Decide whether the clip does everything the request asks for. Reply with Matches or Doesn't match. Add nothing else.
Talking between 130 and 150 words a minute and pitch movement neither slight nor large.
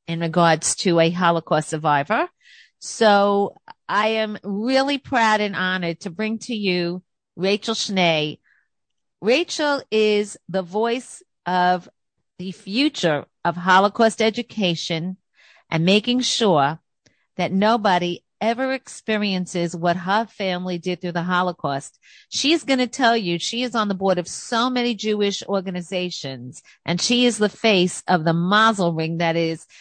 Matches